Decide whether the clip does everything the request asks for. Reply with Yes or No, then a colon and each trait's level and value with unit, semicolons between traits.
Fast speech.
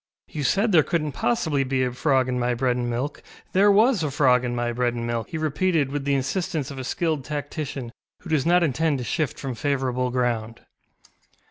Yes: fast, 210 wpm